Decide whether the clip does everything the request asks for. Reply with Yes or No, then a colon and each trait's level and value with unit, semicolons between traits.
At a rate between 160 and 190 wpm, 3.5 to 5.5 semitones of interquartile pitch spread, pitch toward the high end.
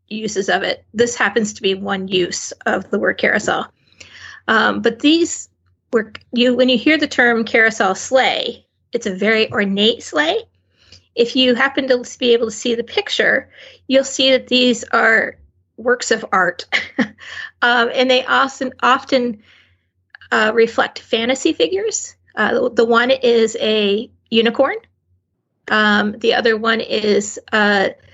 No: average, 150 wpm; average, 3.8 semitones; high, 230 Hz